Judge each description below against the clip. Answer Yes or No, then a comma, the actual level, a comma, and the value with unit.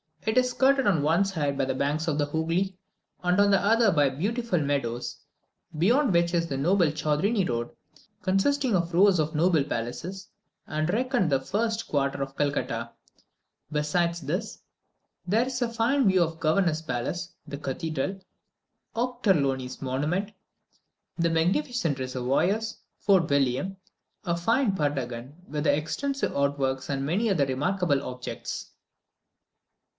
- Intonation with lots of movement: Yes, wide, 5.9 semitones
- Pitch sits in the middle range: Yes, medium, 165 Hz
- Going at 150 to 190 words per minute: No, average, 140 wpm